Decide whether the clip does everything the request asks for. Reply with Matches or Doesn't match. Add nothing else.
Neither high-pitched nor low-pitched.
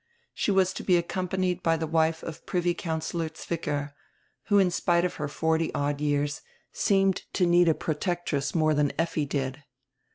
Matches